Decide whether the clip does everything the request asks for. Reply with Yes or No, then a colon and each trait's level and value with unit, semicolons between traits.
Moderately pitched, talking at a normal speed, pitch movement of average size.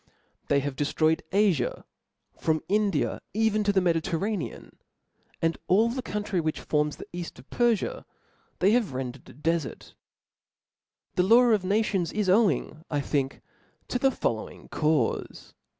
No: medium, 180 Hz; average, 145 wpm; wide, 5.7 semitones